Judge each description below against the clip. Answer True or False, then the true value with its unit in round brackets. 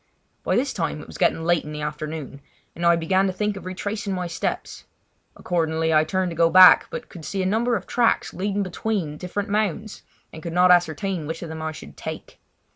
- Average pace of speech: False (215 wpm)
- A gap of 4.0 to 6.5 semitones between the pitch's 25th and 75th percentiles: False (3.6 semitones)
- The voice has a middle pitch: True (180 Hz)